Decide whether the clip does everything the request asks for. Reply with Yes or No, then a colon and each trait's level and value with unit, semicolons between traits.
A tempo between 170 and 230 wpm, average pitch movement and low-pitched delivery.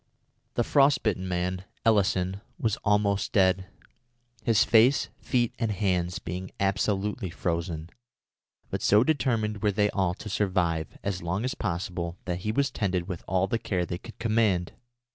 No: average, 155 wpm; average, 3.3 semitones; low, 100 Hz